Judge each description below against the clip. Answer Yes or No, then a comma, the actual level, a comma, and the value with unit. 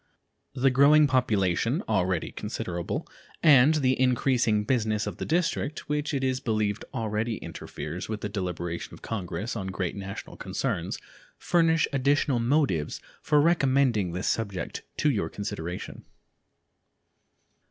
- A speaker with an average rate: No, slow, 125 wpm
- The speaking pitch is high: No, low, 115 Hz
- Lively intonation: Yes, wide, 6.2 semitones